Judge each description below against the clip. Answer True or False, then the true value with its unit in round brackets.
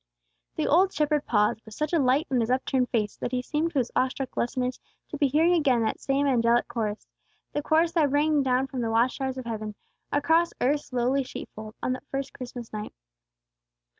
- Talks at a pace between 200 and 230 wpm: True (205 wpm)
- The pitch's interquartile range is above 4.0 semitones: False (3.6 semitones)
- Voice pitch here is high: True (260 Hz)